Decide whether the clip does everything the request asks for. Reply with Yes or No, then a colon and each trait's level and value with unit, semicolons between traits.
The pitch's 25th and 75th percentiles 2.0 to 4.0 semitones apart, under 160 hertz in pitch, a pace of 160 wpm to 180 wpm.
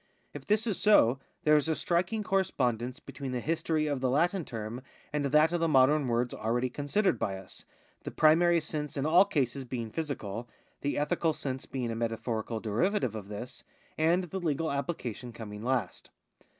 No: average, 5.3 semitones; medium, 140 Hz; average, 175 wpm